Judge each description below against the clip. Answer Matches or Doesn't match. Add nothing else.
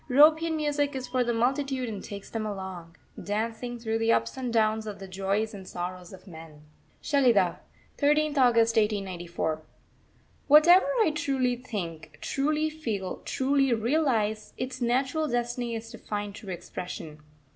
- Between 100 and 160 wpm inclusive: Matches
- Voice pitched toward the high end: Matches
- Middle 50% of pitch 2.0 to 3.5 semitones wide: Doesn't match